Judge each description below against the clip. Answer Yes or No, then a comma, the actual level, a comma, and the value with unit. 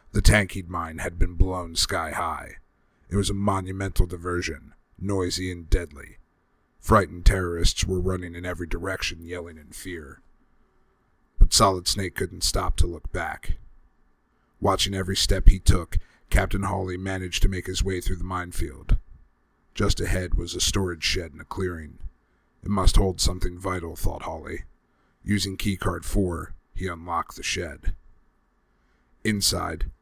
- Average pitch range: No, narrow, 2.0 semitones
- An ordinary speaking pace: Yes, average, 145 wpm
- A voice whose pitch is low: Yes, very low, 90 Hz